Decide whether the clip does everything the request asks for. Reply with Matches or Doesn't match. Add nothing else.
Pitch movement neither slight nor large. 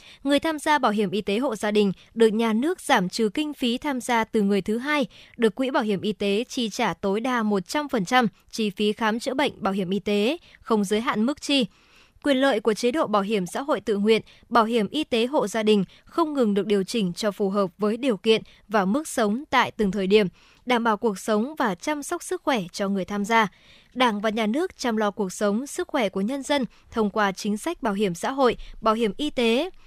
Matches